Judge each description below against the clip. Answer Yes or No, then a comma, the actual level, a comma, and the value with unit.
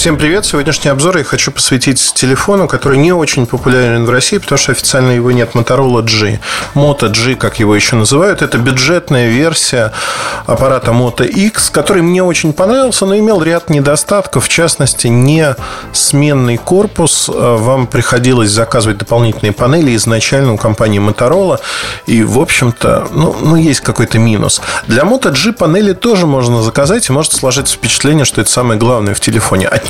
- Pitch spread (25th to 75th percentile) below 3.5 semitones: No, average, 5.0 semitones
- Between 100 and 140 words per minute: No, fast, 160 wpm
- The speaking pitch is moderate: No, low, 130 Hz